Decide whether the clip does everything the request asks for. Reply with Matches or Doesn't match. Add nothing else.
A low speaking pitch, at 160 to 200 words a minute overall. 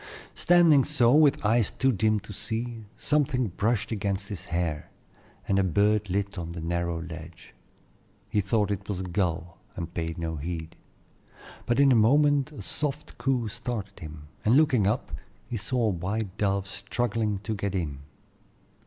Matches